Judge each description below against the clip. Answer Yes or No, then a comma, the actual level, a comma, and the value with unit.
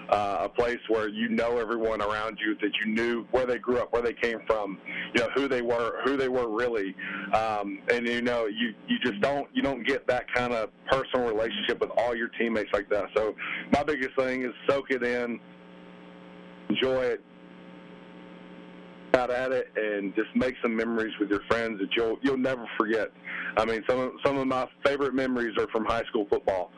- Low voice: Yes, low, 115 Hz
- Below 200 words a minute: No, fast, 205 wpm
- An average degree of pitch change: Yes, average, 3.8 semitones